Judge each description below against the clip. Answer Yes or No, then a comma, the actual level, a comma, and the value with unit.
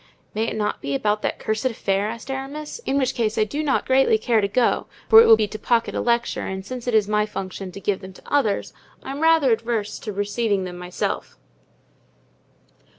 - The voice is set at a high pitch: Yes, high, 220 Hz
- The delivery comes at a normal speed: No, fast, 215 wpm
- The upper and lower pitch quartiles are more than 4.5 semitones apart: No, average, 4.0 semitones